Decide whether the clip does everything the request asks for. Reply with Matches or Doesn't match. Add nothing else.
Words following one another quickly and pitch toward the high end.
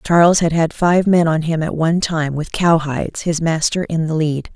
Doesn't match